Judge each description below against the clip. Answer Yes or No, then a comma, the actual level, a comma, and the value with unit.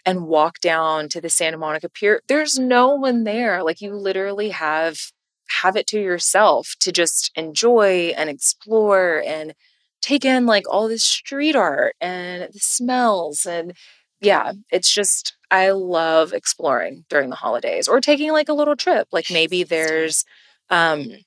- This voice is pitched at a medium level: No, high, 195 Hz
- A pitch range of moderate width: No, wide, 7.1 semitones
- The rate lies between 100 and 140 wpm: No, average, 160 wpm